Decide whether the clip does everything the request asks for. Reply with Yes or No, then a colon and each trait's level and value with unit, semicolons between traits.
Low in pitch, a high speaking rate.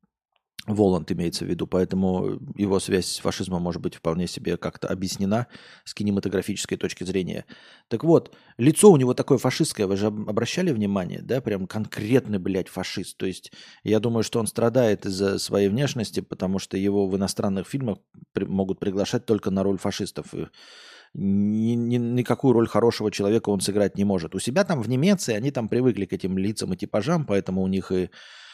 Yes: low, 100 Hz; fast, 180 wpm